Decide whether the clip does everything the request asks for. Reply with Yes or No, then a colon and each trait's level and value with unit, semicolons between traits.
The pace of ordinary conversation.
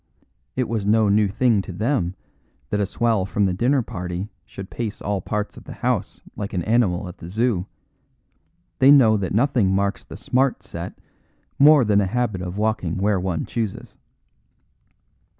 Yes: average, 170 wpm